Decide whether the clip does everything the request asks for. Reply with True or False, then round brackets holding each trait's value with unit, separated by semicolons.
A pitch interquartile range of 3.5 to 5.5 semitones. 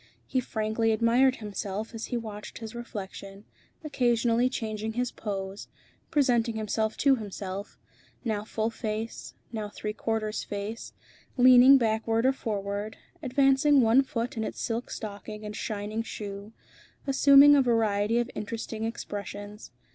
False (2.5 semitones)